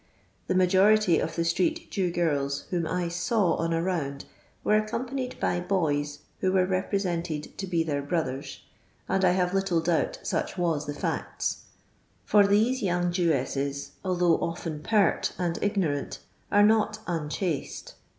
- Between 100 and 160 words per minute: Yes, average, 150 wpm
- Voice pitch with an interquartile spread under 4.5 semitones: Yes, average, 3.5 semitones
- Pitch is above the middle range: No, medium, 175 Hz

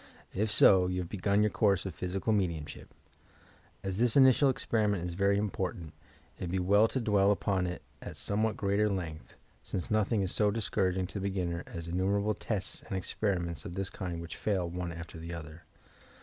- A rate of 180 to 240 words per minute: Yes, average, 195 wpm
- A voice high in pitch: No, very low, 95 Hz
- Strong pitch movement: No, average, 2.8 semitones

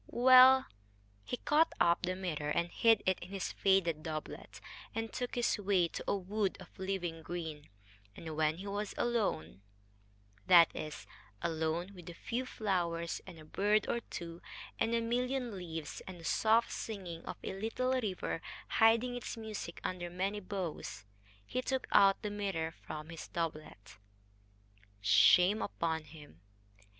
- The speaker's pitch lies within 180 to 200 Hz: Yes, medium, 185 Hz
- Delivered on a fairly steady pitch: No, average, 5.0 semitones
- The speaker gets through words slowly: No, average, 155 wpm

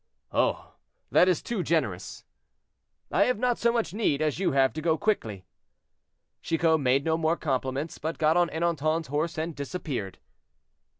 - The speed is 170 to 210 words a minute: No, average, 160 wpm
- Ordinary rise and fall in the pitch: Yes, average, 3.6 semitones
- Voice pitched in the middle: Yes, medium, 160 Hz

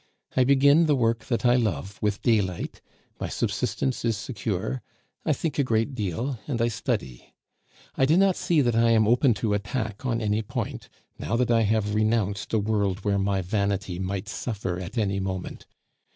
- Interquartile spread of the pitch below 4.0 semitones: Yes, average, 3.5 semitones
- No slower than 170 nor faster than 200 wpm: Yes, average, 180 wpm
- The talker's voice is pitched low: Yes, low, 110 Hz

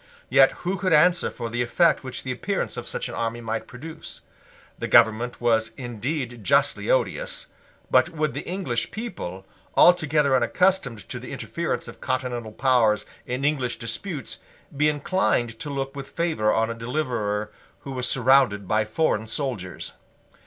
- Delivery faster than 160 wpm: No, average, 155 wpm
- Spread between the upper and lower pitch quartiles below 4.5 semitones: No, average, 4.8 semitones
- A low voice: Yes, low, 130 Hz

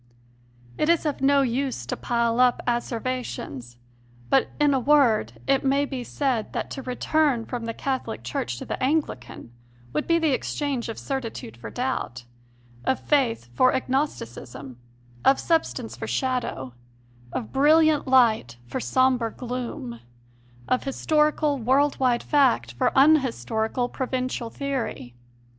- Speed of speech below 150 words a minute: Yes, average, 140 wpm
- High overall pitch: Yes, very high, 255 Hz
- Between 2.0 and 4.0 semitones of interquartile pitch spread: Yes, average, 3.6 semitones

